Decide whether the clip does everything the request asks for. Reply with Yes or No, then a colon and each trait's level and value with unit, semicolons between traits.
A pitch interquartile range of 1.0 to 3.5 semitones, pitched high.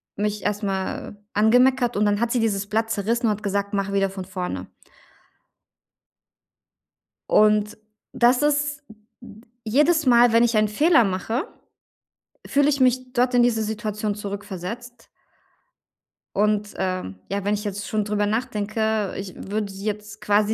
Yes: average, 2.9 semitones; high, 215 Hz